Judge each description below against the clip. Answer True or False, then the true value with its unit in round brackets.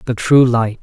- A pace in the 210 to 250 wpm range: True (215 wpm)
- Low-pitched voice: True (120 Hz)